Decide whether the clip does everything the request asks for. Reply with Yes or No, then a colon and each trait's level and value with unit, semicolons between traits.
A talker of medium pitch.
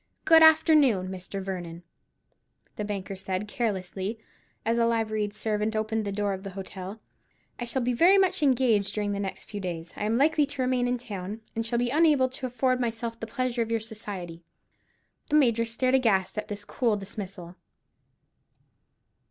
No: high, 220 Hz